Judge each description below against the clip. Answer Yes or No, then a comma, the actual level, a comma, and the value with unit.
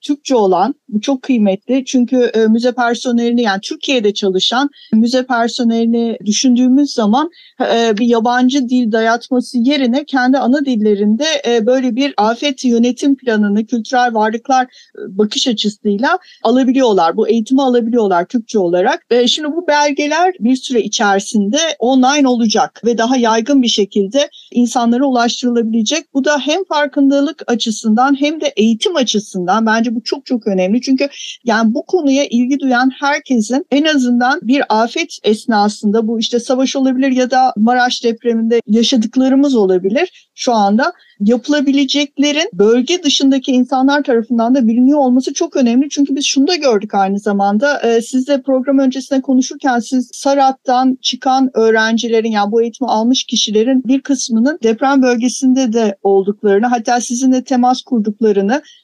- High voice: Yes, very high, 250 Hz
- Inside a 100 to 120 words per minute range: No, average, 135 wpm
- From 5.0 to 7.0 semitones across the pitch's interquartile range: No, average, 3.3 semitones